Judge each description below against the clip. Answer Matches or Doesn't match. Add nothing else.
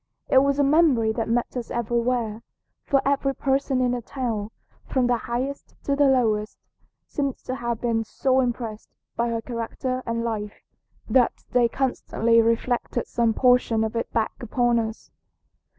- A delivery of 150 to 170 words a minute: Matches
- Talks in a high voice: Matches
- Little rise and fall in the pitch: Matches